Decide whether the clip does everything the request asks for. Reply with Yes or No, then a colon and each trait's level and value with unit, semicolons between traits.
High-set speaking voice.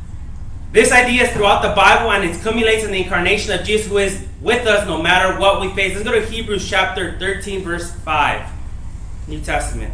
Yes: high, 195 Hz